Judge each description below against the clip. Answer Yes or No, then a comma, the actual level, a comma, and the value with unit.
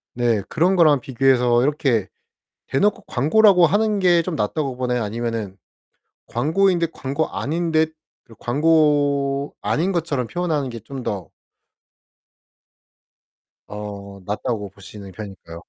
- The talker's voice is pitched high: No, low, 135 Hz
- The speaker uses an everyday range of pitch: No, wide, 6.0 semitones